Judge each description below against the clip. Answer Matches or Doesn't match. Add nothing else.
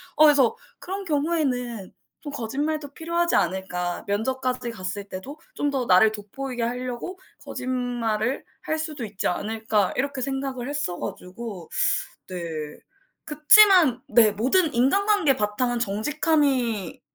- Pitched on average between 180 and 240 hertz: Doesn't match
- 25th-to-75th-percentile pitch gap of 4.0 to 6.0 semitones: Matches